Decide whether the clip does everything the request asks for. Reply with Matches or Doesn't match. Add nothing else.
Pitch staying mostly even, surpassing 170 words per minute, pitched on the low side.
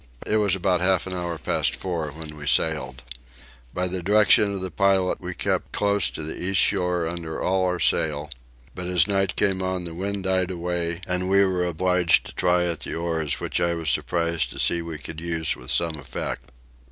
Matches